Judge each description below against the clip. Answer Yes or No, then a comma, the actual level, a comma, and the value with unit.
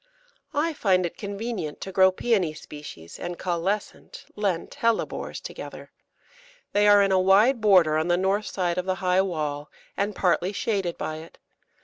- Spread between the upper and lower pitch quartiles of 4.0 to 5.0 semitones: No, average, 3.1 semitones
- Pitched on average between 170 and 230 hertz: Yes, high, 190 Hz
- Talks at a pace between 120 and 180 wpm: Yes, average, 160 wpm